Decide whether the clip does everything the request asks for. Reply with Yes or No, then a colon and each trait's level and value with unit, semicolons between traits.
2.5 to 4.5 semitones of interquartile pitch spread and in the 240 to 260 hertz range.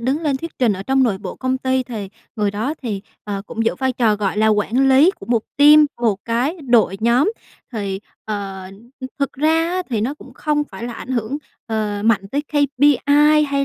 No: average, 5.1 semitones; high, 245 Hz